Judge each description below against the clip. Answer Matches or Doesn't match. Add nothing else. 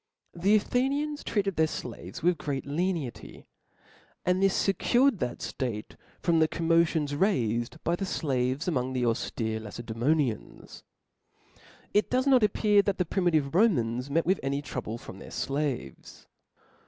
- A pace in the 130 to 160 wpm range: Matches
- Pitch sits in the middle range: Matches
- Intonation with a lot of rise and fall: Matches